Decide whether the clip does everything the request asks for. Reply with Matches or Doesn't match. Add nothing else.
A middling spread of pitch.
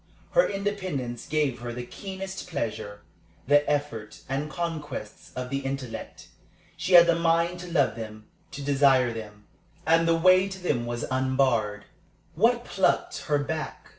Doesn't match